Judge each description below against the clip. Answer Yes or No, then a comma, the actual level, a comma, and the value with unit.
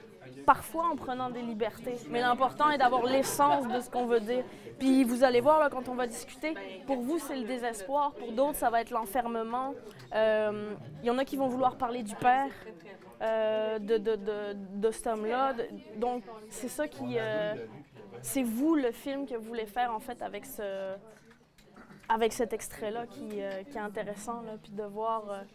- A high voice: Yes, high, 240 Hz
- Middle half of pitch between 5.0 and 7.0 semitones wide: No, average, 3.0 semitones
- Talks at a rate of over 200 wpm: No, average, 195 wpm